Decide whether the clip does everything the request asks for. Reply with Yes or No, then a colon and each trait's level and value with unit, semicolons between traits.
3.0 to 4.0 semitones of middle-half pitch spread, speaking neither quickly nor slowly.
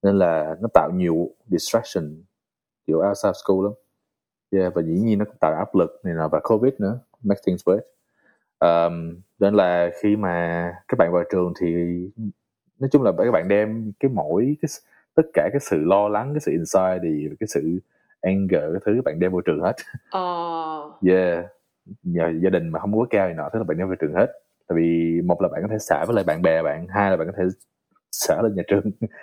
Yes: average, 3.5 semitones; average, 220 wpm